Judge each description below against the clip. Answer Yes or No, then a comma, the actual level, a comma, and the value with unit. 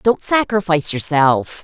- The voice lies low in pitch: No, medium, 175 Hz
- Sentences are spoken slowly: Yes, slow, 110 wpm